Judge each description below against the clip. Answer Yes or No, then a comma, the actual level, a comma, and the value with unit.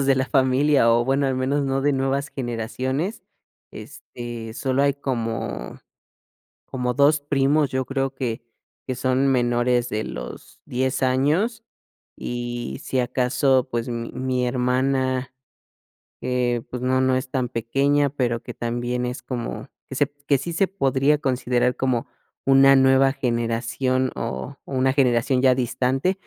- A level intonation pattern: Yes, narrow, 1.8 semitones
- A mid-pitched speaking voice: No, low, 130 Hz